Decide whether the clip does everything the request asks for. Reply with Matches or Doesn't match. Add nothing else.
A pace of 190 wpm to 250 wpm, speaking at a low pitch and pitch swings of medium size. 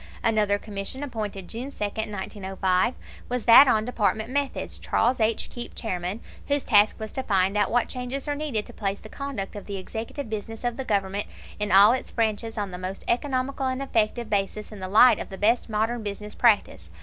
Doesn't match